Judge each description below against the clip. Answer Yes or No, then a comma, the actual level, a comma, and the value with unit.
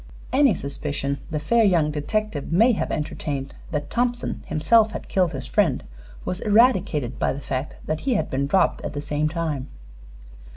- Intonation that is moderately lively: No, wide, 6.8 semitones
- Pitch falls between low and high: Yes, medium, 155 Hz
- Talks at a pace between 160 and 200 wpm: Yes, average, 170 wpm